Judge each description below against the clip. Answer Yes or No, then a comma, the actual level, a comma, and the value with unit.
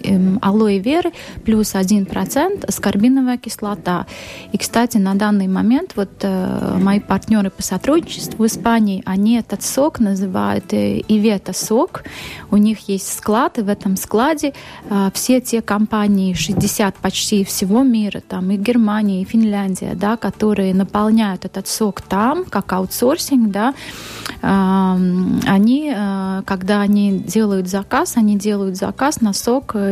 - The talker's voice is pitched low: No, high, 205 Hz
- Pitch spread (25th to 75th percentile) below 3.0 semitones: Yes, narrow, 2.5 semitones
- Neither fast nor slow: Yes, average, 135 wpm